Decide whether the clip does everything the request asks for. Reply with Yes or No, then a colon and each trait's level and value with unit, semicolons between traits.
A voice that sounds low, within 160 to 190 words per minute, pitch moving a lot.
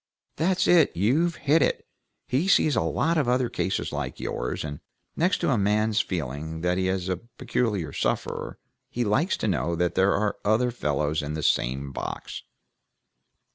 Yes: low, 100 Hz; average, 165 wpm; wide, 7.9 semitones